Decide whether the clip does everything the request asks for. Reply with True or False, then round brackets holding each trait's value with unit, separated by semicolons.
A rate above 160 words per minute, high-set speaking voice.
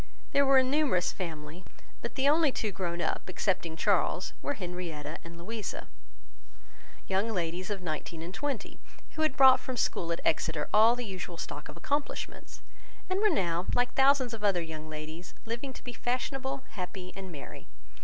True (175 wpm; 195 Hz)